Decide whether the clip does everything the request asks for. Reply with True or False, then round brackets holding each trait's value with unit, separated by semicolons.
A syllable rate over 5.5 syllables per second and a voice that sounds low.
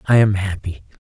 False (5.4 syllables/s; 95 Hz)